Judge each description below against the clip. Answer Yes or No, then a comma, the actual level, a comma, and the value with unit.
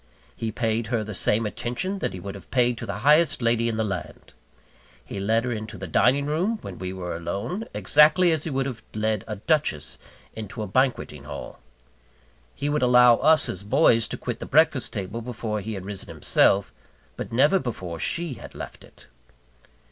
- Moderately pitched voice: No, low, 115 Hz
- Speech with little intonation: No, wide, 5.4 semitones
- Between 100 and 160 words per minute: No, average, 195 wpm